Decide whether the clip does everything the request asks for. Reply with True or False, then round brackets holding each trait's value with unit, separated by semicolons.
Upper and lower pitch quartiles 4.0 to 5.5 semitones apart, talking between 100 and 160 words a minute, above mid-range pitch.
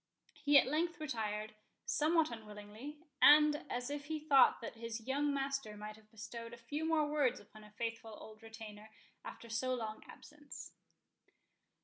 True (5.2 semitones; 155 wpm; 235 Hz)